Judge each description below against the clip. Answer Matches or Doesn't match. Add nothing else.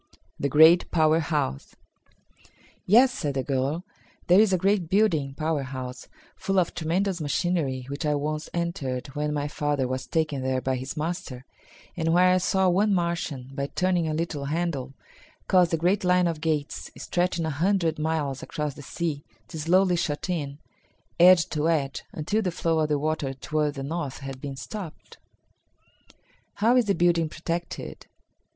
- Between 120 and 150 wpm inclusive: Doesn't match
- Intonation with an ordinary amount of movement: Matches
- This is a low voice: Doesn't match